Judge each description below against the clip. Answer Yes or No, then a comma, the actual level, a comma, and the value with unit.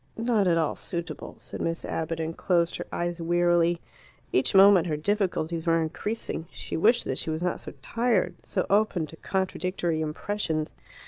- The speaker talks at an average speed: Yes, average, 170 wpm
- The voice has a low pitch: No, medium, 175 Hz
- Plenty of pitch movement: No, average, 3.1 semitones